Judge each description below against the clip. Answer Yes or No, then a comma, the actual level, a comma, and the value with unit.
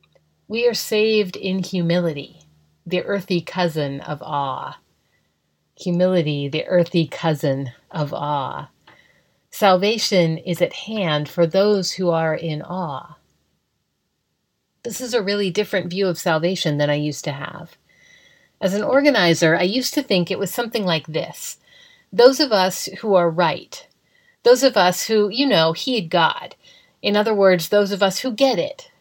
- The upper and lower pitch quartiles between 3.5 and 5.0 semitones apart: Yes, average, 4.6 semitones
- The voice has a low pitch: No, medium, 185 Hz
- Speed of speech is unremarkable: Yes, average, 155 wpm